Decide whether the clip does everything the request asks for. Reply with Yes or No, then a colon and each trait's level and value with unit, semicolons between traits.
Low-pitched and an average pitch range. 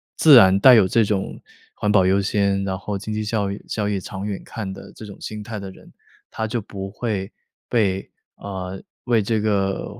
No: low, 100 Hz; narrow, 1.9 semitones